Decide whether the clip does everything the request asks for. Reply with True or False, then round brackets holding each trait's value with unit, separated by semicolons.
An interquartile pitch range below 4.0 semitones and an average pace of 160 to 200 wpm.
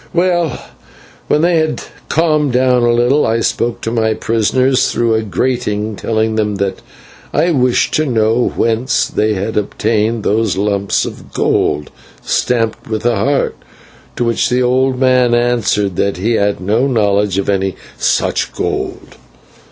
False (3.3 semitones; 150 wpm)